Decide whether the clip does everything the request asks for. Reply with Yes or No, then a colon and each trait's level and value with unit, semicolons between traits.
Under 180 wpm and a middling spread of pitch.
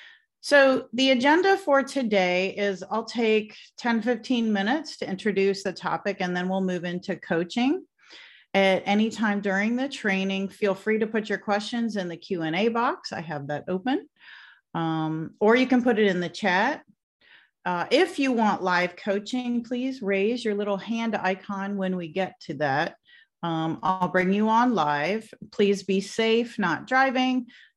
Yes: average, 165 wpm; average, 4.6 semitones